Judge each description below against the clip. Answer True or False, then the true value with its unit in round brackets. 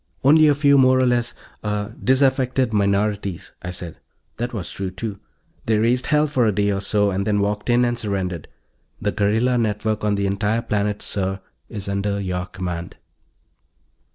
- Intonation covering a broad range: False (3.4 semitones)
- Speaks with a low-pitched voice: True (105 Hz)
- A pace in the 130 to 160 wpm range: False (170 wpm)